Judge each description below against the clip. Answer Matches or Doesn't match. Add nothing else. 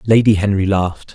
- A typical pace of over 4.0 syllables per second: Matches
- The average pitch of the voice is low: Matches